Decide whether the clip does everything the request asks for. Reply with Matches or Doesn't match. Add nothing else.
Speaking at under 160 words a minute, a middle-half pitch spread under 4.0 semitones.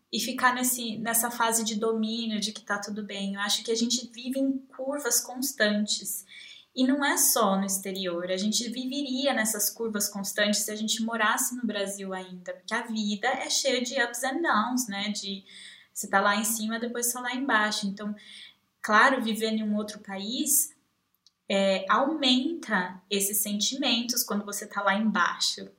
Doesn't match